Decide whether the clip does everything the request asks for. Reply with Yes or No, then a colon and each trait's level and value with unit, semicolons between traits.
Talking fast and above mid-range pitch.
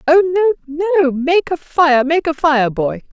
No: average, 190 wpm; very high, 305 Hz